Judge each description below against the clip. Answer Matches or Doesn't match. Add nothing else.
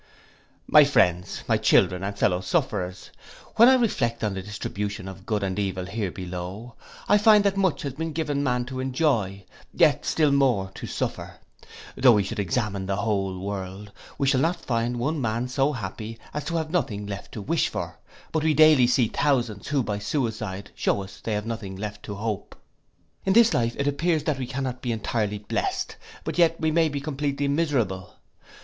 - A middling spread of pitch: Doesn't match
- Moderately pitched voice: Doesn't match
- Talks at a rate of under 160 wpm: Doesn't match